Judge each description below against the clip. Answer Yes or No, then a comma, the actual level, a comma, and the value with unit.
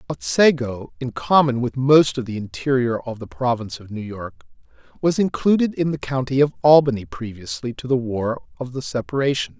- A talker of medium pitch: No, low, 125 Hz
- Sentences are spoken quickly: No, average, 175 wpm